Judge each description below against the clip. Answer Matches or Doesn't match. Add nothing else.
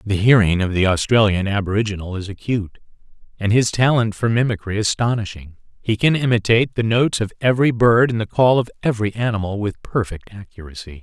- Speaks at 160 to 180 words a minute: Matches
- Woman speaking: Doesn't match